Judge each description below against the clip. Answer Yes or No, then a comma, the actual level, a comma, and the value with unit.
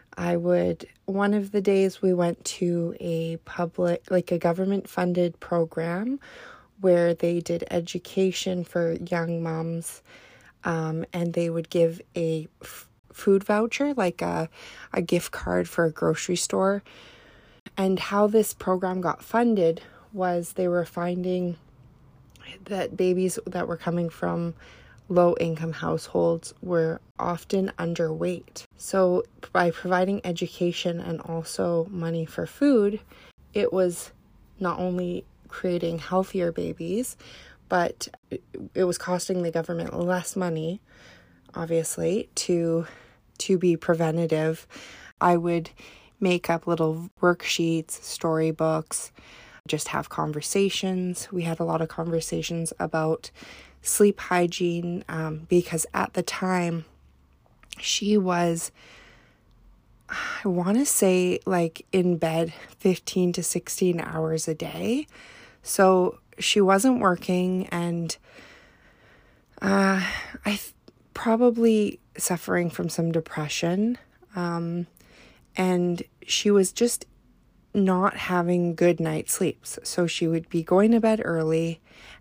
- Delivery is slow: Yes, slow, 115 wpm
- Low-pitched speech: No, medium, 175 Hz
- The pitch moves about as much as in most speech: No, narrow, 2.1 semitones